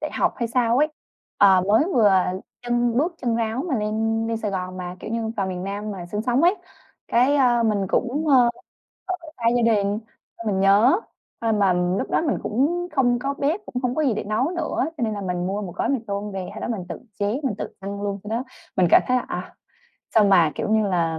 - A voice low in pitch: No, high, 220 Hz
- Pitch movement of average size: Yes, average, 4.0 semitones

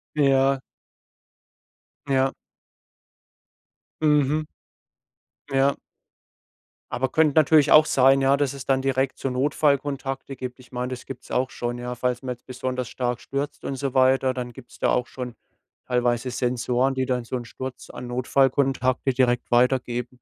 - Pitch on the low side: Yes, low, 130 Hz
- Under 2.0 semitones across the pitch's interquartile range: Yes, narrow, 1.6 semitones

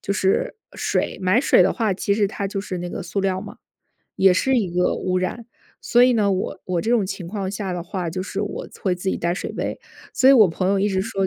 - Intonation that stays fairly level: Yes, narrow, 2.1 semitones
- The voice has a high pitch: Yes, high, 195 Hz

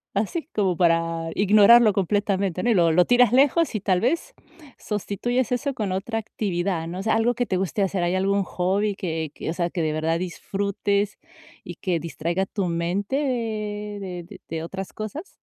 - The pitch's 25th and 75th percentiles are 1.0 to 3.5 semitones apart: No, average, 3.9 semitones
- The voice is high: Yes, high, 200 Hz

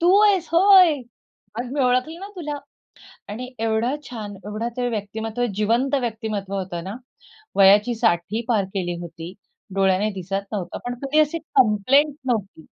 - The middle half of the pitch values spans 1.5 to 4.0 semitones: No, average, 5.2 semitones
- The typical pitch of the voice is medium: No, high, 225 Hz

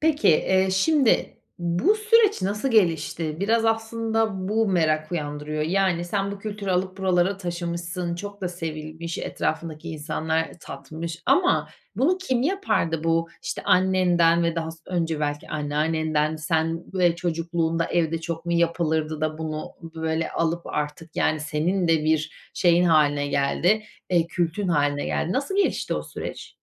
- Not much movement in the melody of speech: No, average, 3.3 semitones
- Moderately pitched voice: Yes, medium, 170 Hz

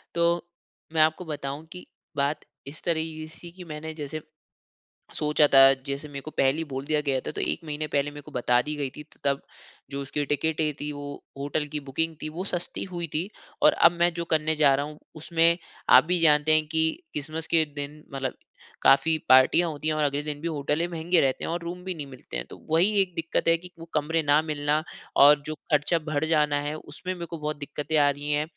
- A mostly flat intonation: Yes, narrow, 2.1 semitones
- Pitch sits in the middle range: Yes, medium, 155 Hz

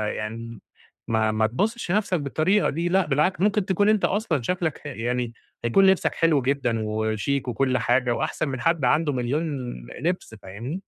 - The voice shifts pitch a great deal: Yes, wide, 6.9 semitones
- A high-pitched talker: No, medium, 140 Hz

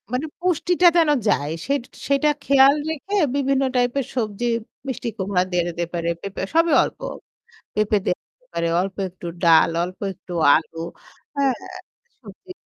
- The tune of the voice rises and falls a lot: Yes, wide, 7.5 semitones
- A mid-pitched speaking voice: No, high, 245 Hz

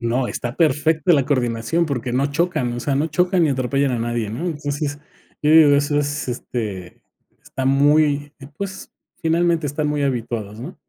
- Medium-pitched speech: Yes, medium, 145 Hz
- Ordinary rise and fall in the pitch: Yes, average, 3.9 semitones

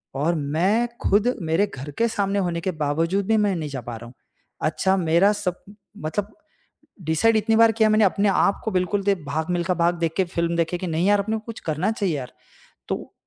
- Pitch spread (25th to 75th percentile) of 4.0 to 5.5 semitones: Yes, average, 4.3 semitones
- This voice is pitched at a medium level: Yes, medium, 180 Hz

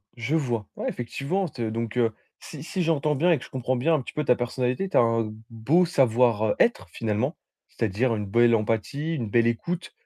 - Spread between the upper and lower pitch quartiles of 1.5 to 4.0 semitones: No, average, 4.8 semitones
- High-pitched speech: No, low, 125 Hz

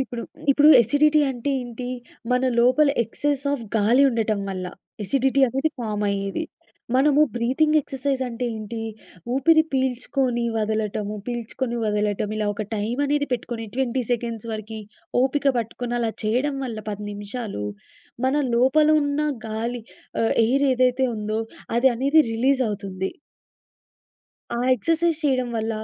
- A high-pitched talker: Yes, high, 245 Hz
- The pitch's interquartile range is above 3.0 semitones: Yes, average, 3.7 semitones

